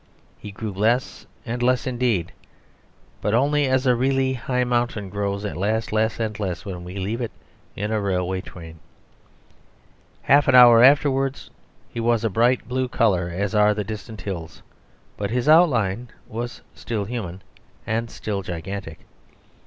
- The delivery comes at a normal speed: Yes, average, 155 wpm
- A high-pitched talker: No, low, 110 Hz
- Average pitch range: Yes, average, 3.9 semitones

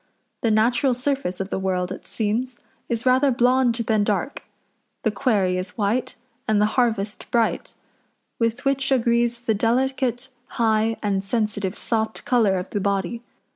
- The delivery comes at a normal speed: Yes, average, 150 wpm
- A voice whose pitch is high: Yes, high, 225 Hz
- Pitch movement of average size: Yes, average, 3.2 semitones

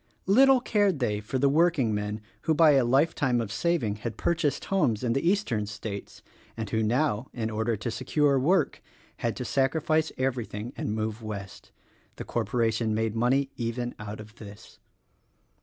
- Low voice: Yes, low, 120 Hz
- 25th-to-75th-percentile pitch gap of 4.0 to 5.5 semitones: Yes, average, 5.2 semitones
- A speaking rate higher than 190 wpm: No, average, 165 wpm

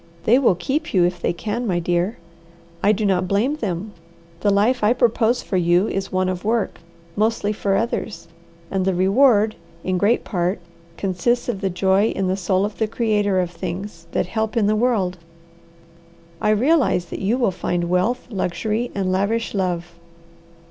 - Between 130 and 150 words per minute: No, average, 175 wpm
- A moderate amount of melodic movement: Yes, average, 3.5 semitones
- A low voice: No, high, 200 Hz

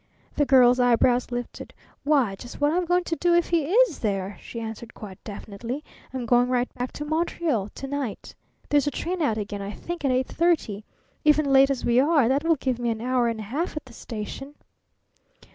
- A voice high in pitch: Yes, very high, 255 Hz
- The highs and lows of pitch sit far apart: No, average, 4.6 semitones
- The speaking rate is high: Yes, fast, 210 wpm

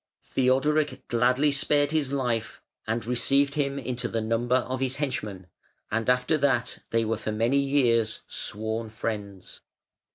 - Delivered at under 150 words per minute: Yes, average, 140 wpm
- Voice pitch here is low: Yes, low, 125 Hz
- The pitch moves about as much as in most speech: Yes, average, 3.5 semitones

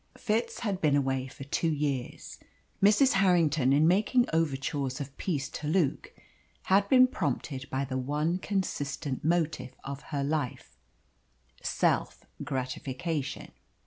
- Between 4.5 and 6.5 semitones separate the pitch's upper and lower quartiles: Yes, average, 4.9 semitones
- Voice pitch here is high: No, medium, 150 Hz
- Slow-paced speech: Yes, slow, 125 wpm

